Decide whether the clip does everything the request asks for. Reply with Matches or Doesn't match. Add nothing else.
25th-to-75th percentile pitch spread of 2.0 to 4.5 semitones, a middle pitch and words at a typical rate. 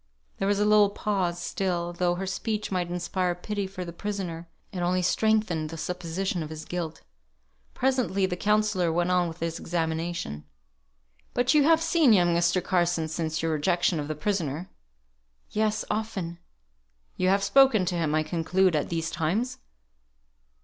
Matches